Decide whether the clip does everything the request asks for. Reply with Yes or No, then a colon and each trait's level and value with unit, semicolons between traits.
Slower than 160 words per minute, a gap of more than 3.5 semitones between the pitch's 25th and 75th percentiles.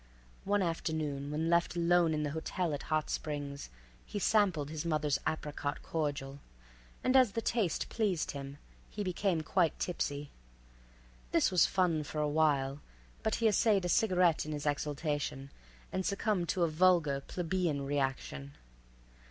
Yes: average, 150 wpm; average, 4.0 semitones